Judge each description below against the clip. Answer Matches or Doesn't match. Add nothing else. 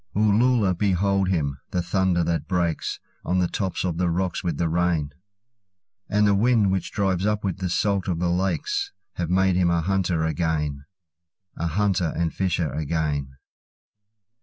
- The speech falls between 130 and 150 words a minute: Matches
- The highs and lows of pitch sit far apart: Doesn't match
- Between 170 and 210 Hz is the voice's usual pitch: Doesn't match